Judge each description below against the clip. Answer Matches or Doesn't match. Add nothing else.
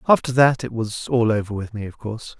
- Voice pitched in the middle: Doesn't match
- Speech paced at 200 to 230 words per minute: Doesn't match